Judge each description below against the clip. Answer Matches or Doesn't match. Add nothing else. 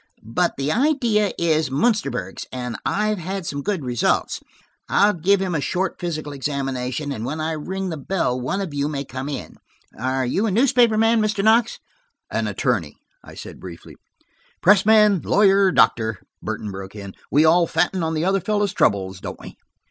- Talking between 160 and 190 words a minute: Matches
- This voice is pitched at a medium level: Matches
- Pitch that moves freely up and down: Matches